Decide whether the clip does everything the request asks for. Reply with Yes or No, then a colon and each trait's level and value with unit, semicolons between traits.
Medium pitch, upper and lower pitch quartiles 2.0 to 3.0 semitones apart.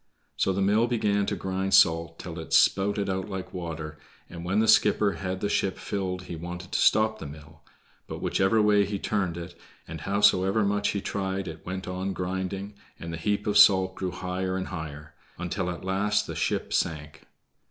No: very low, 95 Hz; average, 2.7 semitones